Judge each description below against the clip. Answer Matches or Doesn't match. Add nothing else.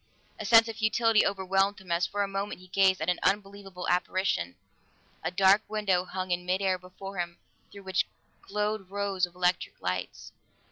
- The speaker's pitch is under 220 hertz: Matches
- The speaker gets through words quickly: Doesn't match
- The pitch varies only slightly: Matches